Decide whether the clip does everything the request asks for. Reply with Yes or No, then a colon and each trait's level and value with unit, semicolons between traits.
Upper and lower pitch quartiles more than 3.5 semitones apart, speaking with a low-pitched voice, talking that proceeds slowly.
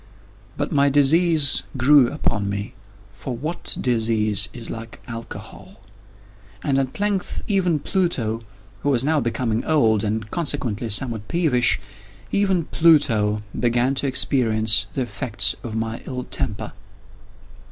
Yes: average, 5.2 semitones; low, 115 Hz; slow, 115 wpm